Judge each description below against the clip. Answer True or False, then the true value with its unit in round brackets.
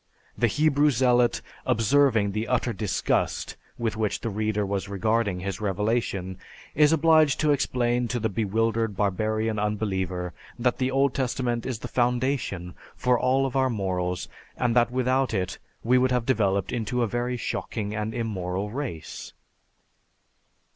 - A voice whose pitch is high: False (115 Hz)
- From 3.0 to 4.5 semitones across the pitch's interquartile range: True (3.7 semitones)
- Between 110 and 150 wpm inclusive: True (145 wpm)